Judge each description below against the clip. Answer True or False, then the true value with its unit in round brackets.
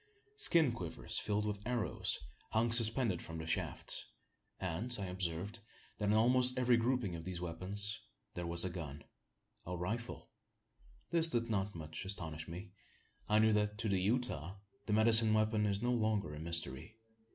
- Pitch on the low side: True (105 Hz)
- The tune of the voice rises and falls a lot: False (4.8 semitones)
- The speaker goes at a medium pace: True (165 wpm)